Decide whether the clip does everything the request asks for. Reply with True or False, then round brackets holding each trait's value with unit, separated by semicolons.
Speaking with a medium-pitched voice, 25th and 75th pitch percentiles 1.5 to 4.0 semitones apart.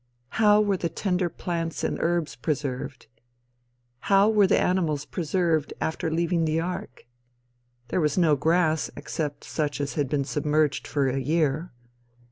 True (160 Hz; 3.3 semitones)